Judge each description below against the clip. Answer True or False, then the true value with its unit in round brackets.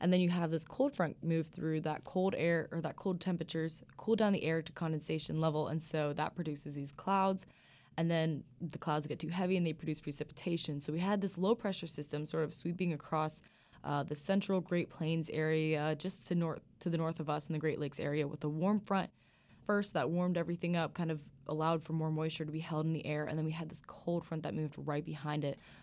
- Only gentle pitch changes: True (2.1 semitones)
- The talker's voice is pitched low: False (160 Hz)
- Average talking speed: False (240 wpm)